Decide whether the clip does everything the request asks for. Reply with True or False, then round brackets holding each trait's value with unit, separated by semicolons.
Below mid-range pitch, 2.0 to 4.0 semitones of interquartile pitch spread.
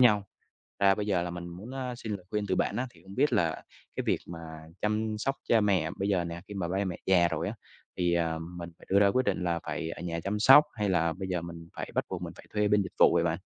True (95 Hz; 3.5 semitones)